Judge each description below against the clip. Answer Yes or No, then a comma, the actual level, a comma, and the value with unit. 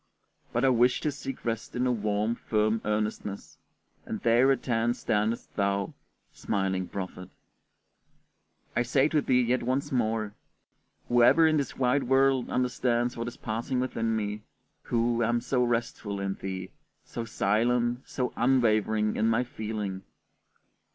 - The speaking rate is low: No, average, 145 wpm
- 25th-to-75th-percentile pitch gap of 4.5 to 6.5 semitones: No, average, 2.7 semitones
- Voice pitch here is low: Yes, low, 115 Hz